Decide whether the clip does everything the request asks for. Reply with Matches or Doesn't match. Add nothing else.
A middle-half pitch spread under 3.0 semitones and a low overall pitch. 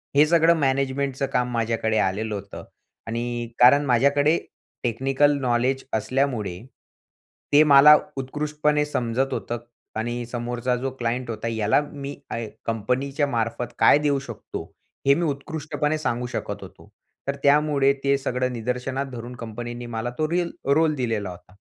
Doesn't match